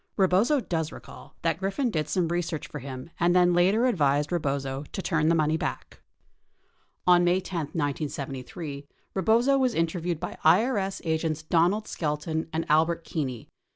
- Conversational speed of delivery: Yes, average, 160 wpm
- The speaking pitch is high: No, medium, 165 Hz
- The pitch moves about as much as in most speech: Yes, average, 3.4 semitones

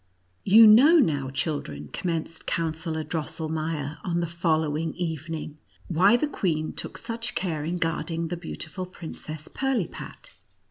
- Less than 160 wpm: Yes, average, 140 wpm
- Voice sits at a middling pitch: Yes, medium, 165 Hz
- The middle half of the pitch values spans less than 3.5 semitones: Yes, narrow, 2.6 semitones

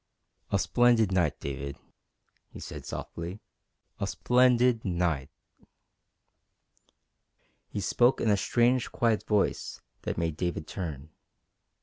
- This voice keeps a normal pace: No, slow, 105 wpm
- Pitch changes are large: Yes, wide, 6.4 semitones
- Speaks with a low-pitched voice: Yes, very low, 95 Hz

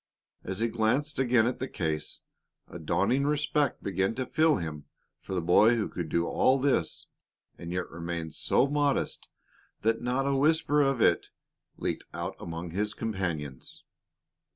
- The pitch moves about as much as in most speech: No, wide, 7.9 semitones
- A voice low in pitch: Yes, low, 110 Hz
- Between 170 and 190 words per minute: No, average, 155 wpm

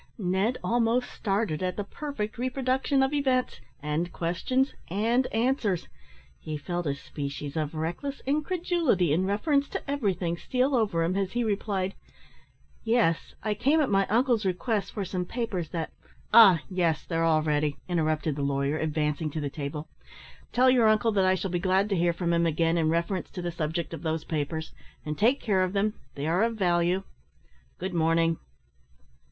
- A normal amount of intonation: No, wide, 5.9 semitones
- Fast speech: No, average, 175 wpm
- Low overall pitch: No, medium, 185 Hz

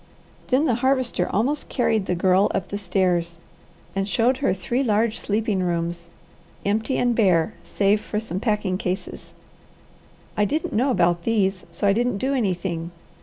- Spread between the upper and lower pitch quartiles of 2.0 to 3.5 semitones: No, average, 4.4 semitones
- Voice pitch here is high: Yes, high, 205 Hz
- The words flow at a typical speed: Yes, average, 160 wpm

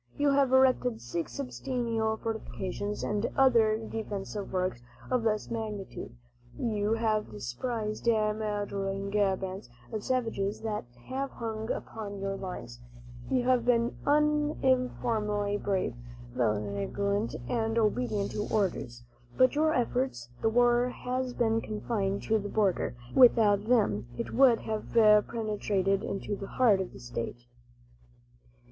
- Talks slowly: Yes, slow, 125 wpm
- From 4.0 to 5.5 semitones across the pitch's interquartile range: No, average, 3.4 semitones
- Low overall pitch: No, high, 215 Hz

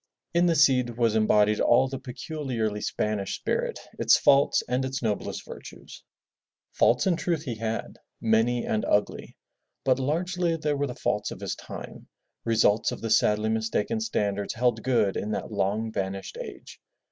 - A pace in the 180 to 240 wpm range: No, average, 165 wpm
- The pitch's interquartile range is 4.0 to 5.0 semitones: Yes, average, 4.3 semitones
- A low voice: Yes, low, 115 Hz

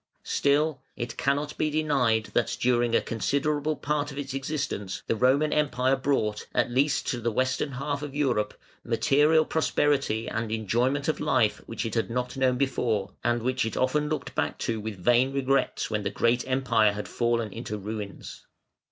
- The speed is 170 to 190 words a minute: Yes, average, 175 wpm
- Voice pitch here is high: No, low, 130 Hz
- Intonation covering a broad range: No, average, 3.9 semitones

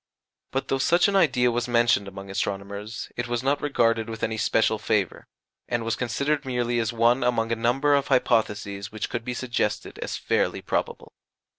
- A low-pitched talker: Yes, low, 120 Hz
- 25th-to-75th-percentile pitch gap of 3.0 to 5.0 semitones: No, narrow, 2.6 semitones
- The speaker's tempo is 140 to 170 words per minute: No, average, 180 wpm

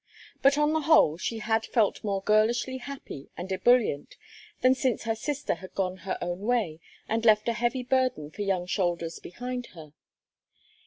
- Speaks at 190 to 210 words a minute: No, average, 170 wpm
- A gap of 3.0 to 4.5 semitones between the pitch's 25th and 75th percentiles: No, average, 5.2 semitones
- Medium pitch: No, high, 220 Hz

